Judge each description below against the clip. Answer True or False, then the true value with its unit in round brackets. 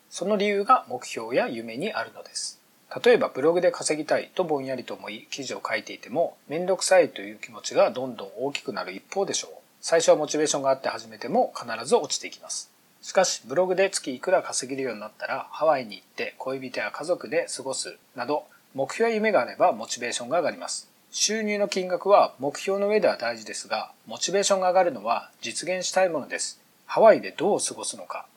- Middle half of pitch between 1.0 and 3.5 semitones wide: False (5.1 semitones)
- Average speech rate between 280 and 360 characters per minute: False (440 characters per minute)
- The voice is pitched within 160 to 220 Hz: True (185 Hz)